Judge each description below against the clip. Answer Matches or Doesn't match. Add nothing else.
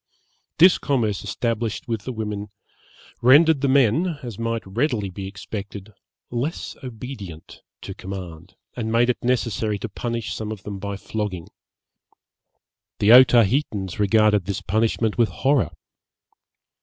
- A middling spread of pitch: Matches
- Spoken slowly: Matches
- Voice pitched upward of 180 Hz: Doesn't match